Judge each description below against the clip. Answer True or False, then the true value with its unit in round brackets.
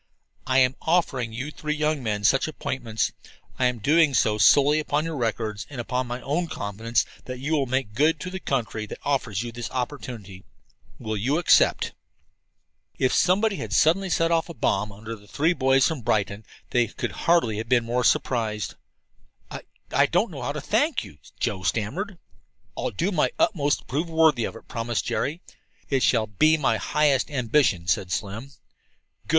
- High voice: False (125 Hz)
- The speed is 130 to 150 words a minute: False (180 wpm)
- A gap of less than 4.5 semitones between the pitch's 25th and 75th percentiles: False (5.5 semitones)